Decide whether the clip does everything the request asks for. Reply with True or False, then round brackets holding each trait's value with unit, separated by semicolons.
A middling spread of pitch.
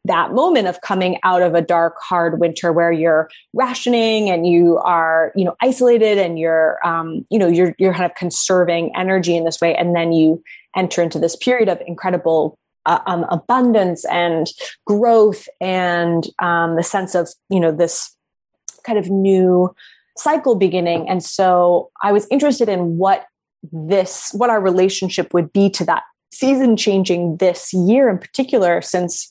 True (3.2 semitones)